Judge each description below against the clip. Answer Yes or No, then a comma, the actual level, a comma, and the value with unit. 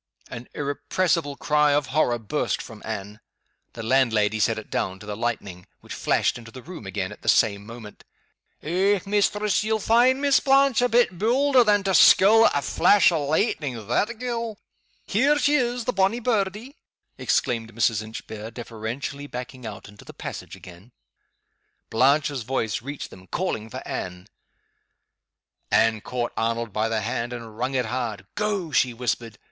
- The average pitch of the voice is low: Yes, low, 130 Hz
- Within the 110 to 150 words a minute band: No, average, 165 wpm